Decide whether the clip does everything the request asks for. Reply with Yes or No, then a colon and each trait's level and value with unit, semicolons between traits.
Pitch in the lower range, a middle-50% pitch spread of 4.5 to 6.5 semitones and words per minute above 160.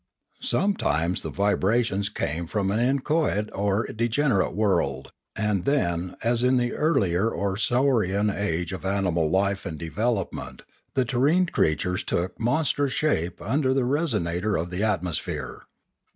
No: low, 100 Hz; wide, 5.5 semitones; average, 145 wpm